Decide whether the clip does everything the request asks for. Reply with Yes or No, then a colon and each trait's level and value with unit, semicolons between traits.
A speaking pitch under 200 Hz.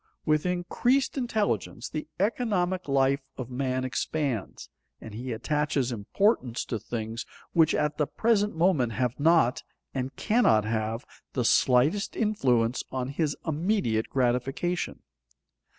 Yes: medium, 140 Hz